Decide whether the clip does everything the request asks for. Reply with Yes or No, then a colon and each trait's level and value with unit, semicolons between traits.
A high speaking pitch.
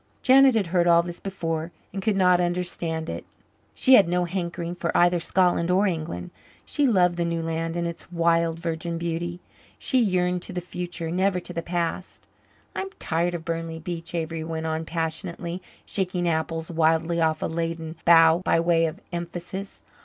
No: medium, 170 Hz